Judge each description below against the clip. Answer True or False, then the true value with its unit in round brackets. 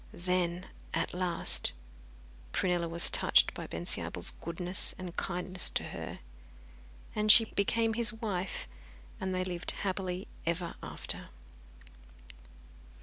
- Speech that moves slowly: True (110 wpm)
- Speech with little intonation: True (2.1 semitones)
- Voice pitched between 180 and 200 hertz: True (185 Hz)